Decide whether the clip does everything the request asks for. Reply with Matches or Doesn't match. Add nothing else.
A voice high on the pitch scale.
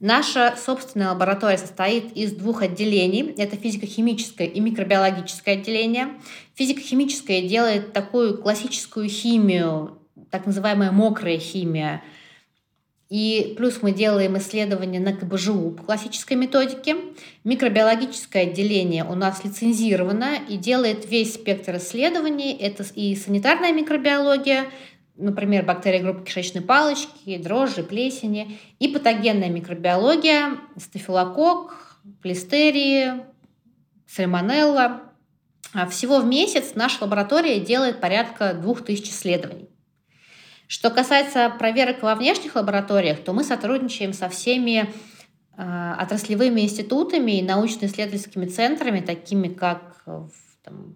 Matches